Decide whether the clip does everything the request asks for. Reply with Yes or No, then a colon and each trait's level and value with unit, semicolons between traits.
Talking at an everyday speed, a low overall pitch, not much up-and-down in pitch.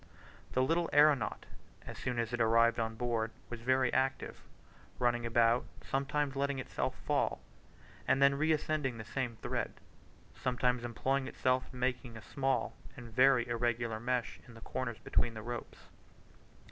Yes: average, 150 wpm; low, 125 Hz; narrow, 2.3 semitones